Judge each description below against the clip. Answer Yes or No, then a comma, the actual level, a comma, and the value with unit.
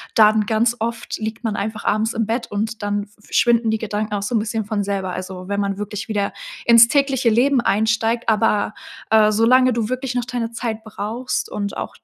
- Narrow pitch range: Yes, narrow, 2.1 semitones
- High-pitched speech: Yes, high, 220 Hz